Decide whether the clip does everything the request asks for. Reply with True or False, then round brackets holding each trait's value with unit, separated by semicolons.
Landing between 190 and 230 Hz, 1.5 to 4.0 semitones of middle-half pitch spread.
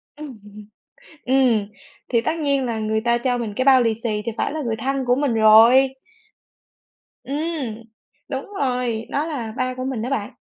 False (250 Hz; 3.1 semitones)